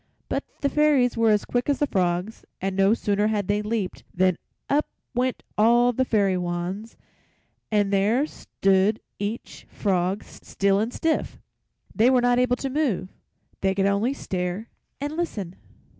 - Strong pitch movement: No, average, 4.2 semitones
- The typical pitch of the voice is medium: No, high, 210 Hz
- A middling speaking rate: Yes, average, 160 wpm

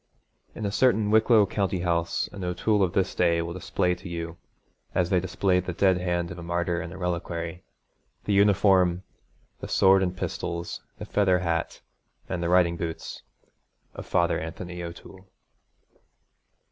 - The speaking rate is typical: Yes, average, 160 wpm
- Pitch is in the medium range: No, very low, 90 Hz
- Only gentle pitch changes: Yes, narrow, 2.0 semitones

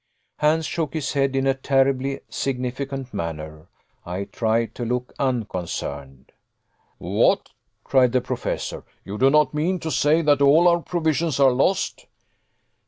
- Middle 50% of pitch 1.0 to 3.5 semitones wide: No, average, 4.4 semitones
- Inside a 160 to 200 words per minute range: No, average, 140 wpm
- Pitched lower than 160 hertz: Yes, low, 135 Hz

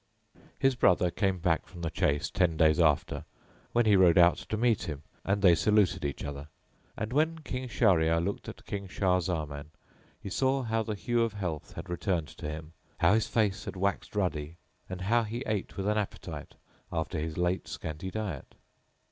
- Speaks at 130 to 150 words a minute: No, average, 190 wpm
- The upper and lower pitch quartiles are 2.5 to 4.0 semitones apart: No, average, 4.7 semitones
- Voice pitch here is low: Yes, very low, 95 Hz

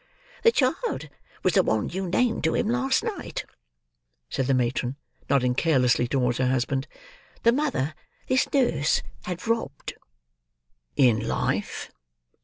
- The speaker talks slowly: Yes, slow, 130 wpm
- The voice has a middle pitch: Yes, medium, 155 Hz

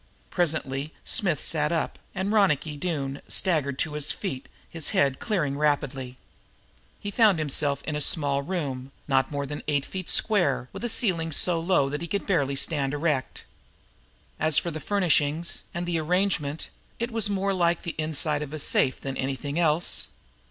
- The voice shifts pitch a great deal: No, average, 3.9 semitones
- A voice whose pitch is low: No, medium, 155 Hz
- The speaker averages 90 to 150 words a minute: No, average, 170 wpm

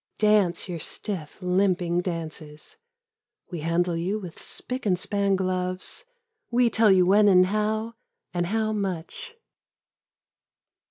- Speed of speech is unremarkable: No, slow, 120 wpm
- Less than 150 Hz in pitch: No, medium, 185 Hz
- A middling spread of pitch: Yes, average, 3.4 semitones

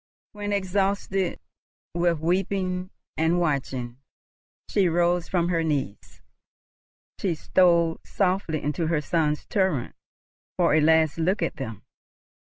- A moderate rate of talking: No, slow, 115 wpm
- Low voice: No, medium, 170 Hz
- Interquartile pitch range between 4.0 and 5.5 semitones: No, average, 3.0 semitones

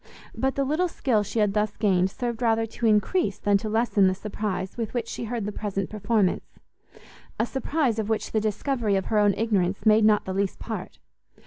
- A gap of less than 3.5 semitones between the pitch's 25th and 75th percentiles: Yes, narrow, 2.5 semitones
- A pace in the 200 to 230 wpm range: Yes, fast, 205 wpm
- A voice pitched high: Yes, high, 215 Hz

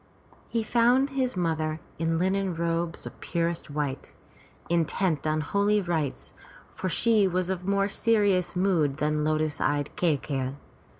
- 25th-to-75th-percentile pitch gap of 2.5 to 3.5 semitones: No, average, 4.2 semitones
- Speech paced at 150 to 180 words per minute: No, average, 140 wpm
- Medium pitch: Yes, medium, 170 Hz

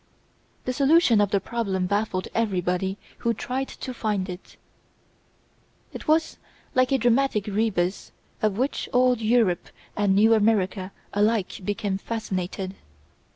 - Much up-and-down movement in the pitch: No, average, 3.9 semitones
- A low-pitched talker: No, high, 210 Hz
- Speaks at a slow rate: Yes, slow, 125 wpm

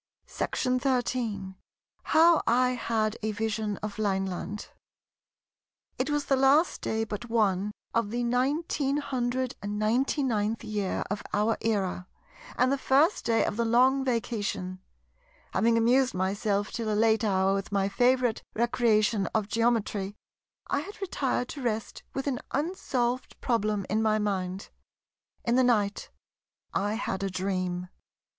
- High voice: Yes, high, 225 Hz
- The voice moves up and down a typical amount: Yes, average, 3.7 semitones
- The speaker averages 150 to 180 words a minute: No, slow, 135 wpm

